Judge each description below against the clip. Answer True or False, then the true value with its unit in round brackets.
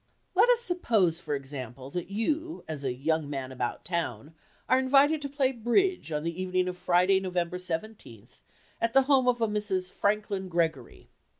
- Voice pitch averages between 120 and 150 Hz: False (185 Hz)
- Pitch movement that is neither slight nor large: False (7.7 semitones)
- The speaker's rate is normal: True (170 wpm)